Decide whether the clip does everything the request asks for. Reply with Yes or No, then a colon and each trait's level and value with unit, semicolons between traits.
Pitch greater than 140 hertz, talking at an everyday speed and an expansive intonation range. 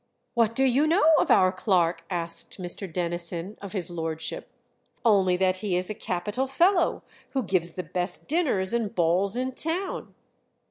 Yes: high, 190 Hz; average, 165 wpm; wide, 6.0 semitones